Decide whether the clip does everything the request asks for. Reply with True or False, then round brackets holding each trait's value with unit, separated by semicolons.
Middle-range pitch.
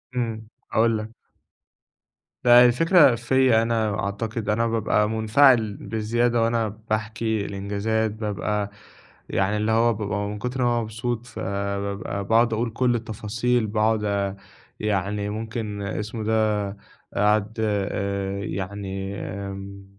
False (110 Hz)